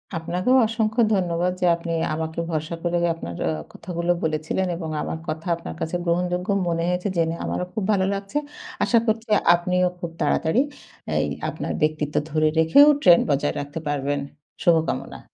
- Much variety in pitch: No, narrow, 2.4 semitones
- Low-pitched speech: No, medium, 170 Hz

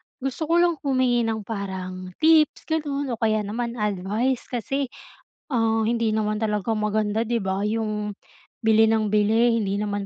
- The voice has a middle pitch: No, high, 220 Hz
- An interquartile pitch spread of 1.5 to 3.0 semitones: Yes, narrow, 2.5 semitones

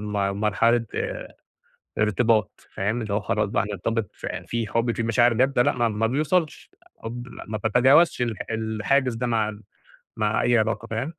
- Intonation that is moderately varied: No, narrow, 2.3 semitones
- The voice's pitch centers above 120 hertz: No, low, 115 Hz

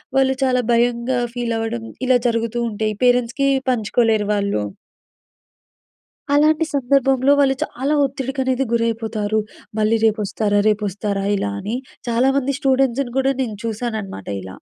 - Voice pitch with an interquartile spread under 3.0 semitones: No, average, 3.5 semitones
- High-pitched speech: Yes, high, 235 Hz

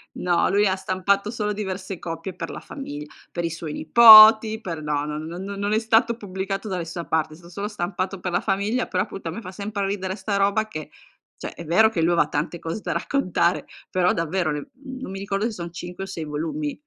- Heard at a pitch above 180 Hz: Yes, high, 190 Hz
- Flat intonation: No, average, 3.6 semitones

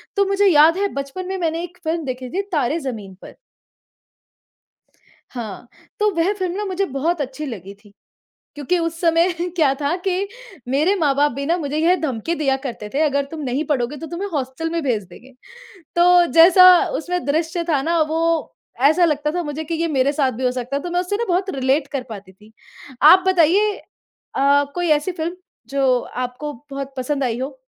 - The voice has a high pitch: Yes, very high, 305 Hz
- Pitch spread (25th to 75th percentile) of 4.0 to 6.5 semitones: Yes, average, 4.6 semitones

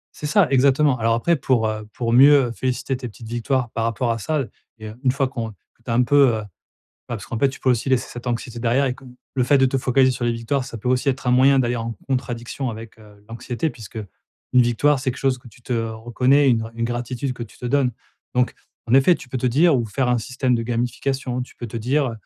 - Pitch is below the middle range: Yes, low, 125 Hz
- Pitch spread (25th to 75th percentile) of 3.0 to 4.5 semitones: No, narrow, 2.4 semitones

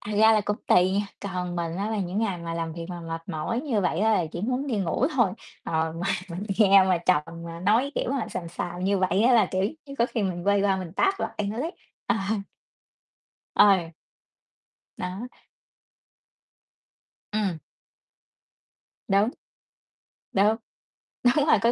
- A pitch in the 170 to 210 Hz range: Yes, high, 195 Hz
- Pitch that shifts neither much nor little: Yes, average, 3.9 semitones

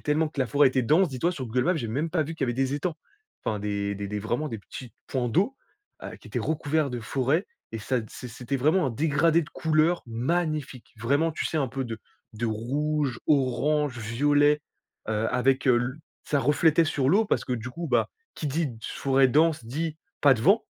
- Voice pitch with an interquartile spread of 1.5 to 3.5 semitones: No, average, 4.3 semitones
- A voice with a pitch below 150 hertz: Yes, medium, 140 Hz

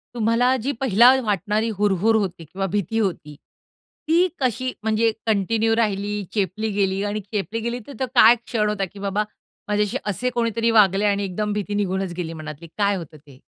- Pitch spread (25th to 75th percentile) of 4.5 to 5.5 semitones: No, average, 2.7 semitones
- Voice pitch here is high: Yes, high, 210 Hz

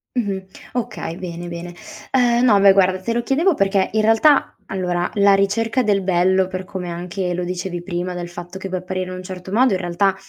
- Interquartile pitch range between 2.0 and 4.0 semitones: Yes, narrow, 2.5 semitones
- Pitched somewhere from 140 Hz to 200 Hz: Yes, high, 190 Hz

